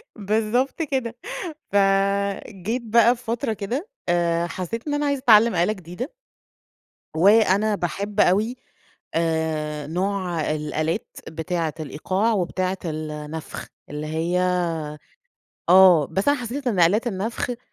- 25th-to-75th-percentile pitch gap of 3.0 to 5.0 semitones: No, wide, 5.5 semitones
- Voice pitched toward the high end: Yes, high, 195 Hz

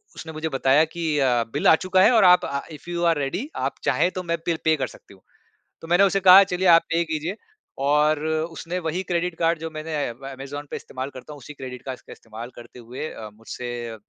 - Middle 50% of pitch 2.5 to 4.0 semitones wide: No, average, 4.6 semitones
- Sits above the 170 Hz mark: No, medium, 155 Hz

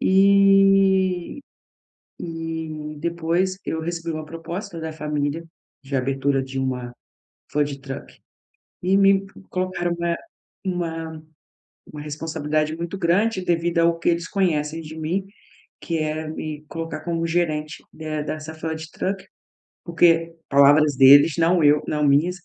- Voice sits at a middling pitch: Yes, medium, 165 Hz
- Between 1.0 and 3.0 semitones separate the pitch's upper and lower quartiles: Yes, narrow, 2.4 semitones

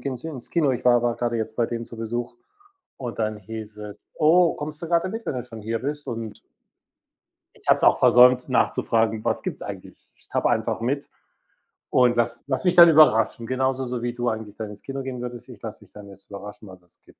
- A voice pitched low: Yes, low, 120 Hz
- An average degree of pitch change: Yes, average, 3.3 semitones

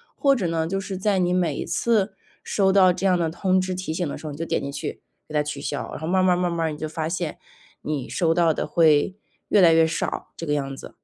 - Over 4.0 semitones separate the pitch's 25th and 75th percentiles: No, average, 3.2 semitones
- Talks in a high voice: No, medium, 170 Hz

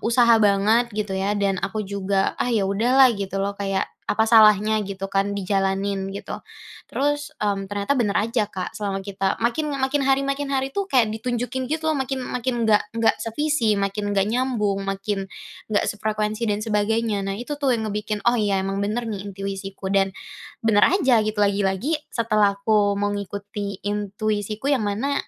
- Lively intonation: No, average, 3.2 semitones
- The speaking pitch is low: No, high, 210 Hz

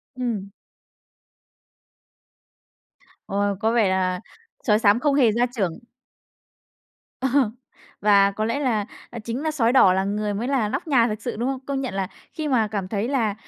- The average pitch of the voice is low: No, high, 220 Hz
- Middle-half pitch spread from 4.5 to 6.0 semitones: No, average, 4.0 semitones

